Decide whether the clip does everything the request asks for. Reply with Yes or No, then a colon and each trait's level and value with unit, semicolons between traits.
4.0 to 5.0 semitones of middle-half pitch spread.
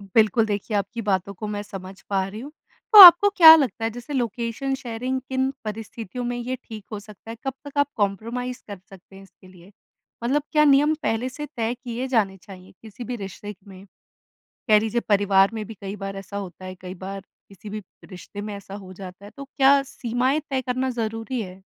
Yes: average, 4.3 semitones